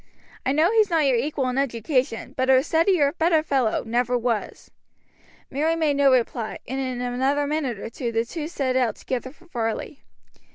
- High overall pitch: Yes, very high, 265 Hz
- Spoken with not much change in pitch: No, average, 3.7 semitones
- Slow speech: No, average, 170 wpm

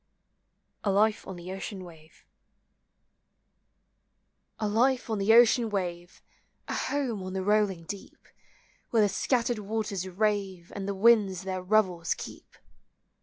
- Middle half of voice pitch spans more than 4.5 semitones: No, average, 2.7 semitones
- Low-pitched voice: No, high, 200 Hz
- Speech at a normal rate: No, slow, 130 wpm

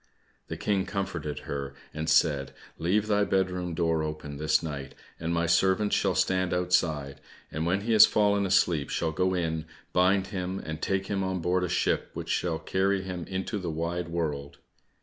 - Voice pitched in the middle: No, very low, 90 Hz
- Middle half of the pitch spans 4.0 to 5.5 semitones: No, average, 3.2 semitones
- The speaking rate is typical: Yes, average, 185 wpm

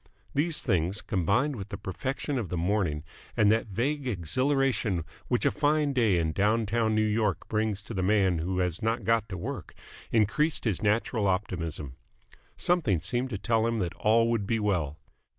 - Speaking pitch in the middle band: No, low, 105 Hz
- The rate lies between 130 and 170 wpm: No, average, 180 wpm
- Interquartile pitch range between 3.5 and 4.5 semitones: Yes, average, 4.1 semitones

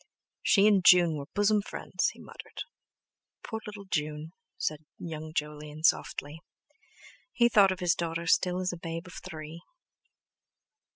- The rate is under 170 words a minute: Yes, average, 140 wpm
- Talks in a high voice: No, medium, 170 Hz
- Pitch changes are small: No, average, 3.5 semitones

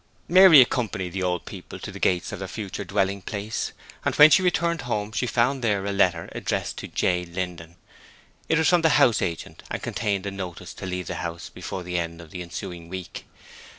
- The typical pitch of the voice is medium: No, very low, 95 Hz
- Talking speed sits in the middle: No, fast, 210 wpm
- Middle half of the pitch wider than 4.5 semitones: Yes, average, 5.2 semitones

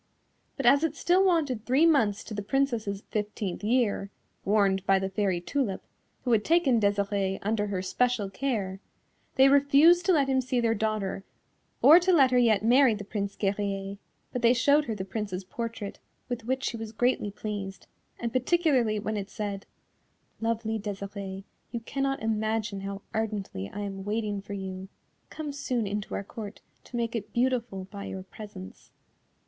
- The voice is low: No, high, 215 Hz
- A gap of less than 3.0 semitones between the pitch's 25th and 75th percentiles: No, average, 4.1 semitones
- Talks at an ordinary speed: Yes, average, 170 wpm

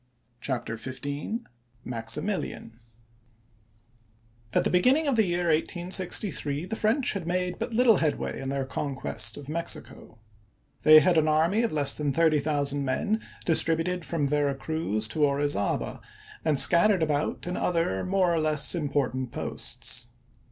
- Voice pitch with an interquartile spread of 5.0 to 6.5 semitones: Yes, average, 5.3 semitones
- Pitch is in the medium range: Yes, medium, 150 Hz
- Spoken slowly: No, average, 155 wpm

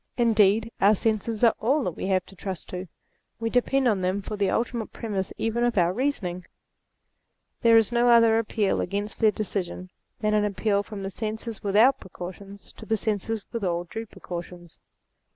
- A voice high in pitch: Yes, high, 210 Hz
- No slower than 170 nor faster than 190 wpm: Yes, average, 180 wpm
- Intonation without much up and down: No, average, 3.0 semitones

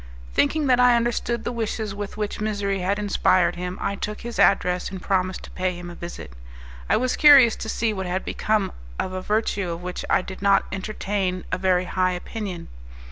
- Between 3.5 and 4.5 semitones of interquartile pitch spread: No, average, 3.0 semitones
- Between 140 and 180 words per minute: No, average, 200 wpm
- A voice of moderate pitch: No, high, 195 Hz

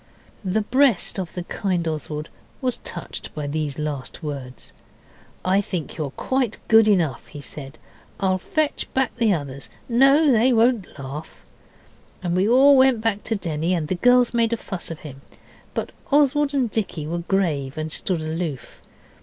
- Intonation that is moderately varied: No, wide, 7.4 semitones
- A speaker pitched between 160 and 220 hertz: Yes, medium, 185 Hz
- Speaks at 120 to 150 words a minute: No, average, 165 wpm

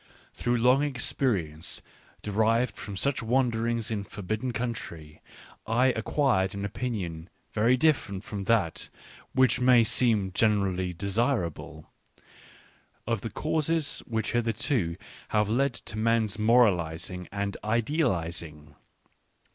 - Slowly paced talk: Yes, slow, 115 wpm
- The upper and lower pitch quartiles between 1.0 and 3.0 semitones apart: No, average, 4.3 semitones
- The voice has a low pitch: Yes, low, 110 Hz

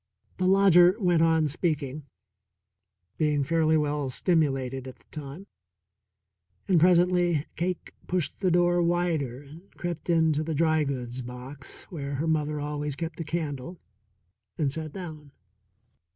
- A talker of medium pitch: Yes, medium, 155 Hz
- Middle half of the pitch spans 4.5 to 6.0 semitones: No, average, 3.4 semitones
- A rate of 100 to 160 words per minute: Yes, slow, 135 wpm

